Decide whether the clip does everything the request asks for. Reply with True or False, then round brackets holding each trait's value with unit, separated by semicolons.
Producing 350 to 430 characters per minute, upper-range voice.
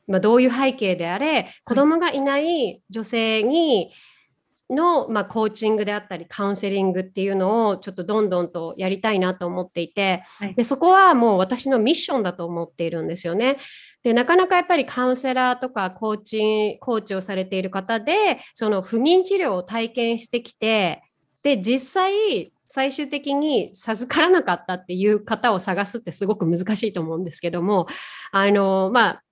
True (370 characters per minute; 220 Hz)